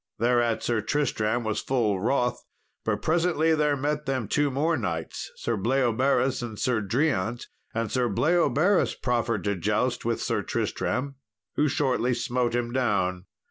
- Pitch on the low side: Yes, low, 125 Hz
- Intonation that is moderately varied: Yes, average, 4.0 semitones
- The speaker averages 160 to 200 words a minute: No, average, 145 wpm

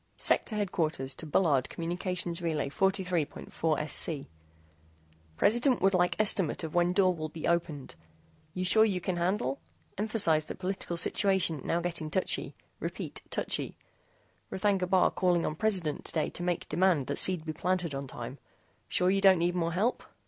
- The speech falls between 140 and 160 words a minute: Yes, average, 150 wpm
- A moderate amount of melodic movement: Yes, average, 3.1 semitones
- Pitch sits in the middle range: Yes, medium, 175 Hz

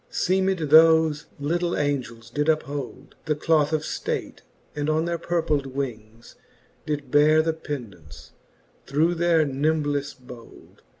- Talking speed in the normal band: No, slow, 130 wpm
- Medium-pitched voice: Yes, medium, 150 Hz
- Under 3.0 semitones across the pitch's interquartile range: Yes, narrow, 2.6 semitones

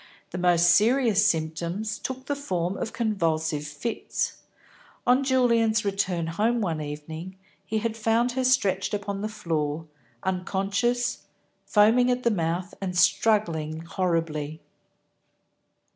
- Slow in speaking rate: Yes, slow, 120 wpm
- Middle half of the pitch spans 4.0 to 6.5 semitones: Yes, wide, 5.5 semitones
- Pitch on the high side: Yes, high, 195 Hz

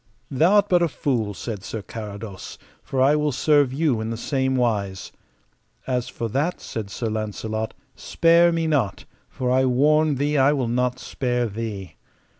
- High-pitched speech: No, low, 125 Hz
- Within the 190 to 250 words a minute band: No, average, 170 wpm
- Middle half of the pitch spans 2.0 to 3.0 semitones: No, average, 4.9 semitones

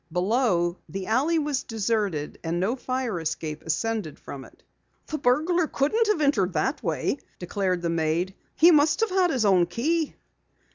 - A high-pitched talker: Yes, high, 225 Hz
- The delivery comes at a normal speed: Yes, average, 160 wpm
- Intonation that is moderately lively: No, wide, 9.0 semitones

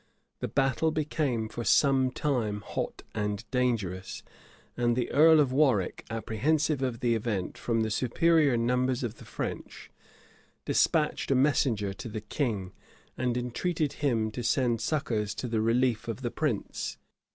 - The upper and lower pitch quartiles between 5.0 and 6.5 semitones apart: No, average, 3.7 semitones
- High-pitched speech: No, low, 125 Hz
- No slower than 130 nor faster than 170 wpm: Yes, average, 150 wpm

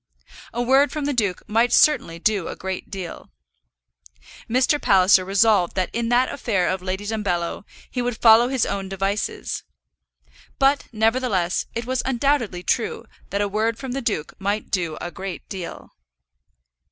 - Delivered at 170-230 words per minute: No, average, 155 wpm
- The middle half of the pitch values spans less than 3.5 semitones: No, average, 4.4 semitones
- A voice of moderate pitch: No, high, 215 Hz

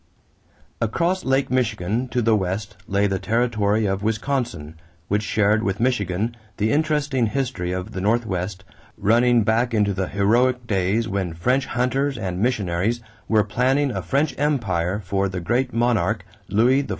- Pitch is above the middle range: No, low, 110 Hz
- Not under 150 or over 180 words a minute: Yes, average, 155 wpm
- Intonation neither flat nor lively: Yes, average, 4.2 semitones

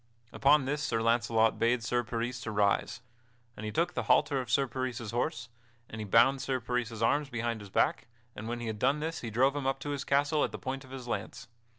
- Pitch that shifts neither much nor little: Yes, average, 3.1 semitones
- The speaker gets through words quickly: Yes, fast, 230 wpm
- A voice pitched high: No, low, 120 Hz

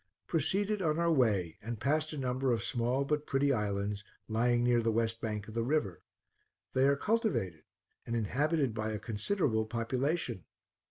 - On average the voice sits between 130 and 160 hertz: No, low, 120 Hz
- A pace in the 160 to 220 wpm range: Yes, average, 165 wpm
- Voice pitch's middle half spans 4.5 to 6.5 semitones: Yes, average, 5.2 semitones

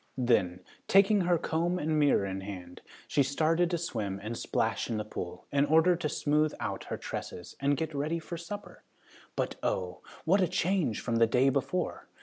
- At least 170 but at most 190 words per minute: Yes, average, 185 wpm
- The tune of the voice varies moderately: No, wide, 7.9 semitones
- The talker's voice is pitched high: No, medium, 145 Hz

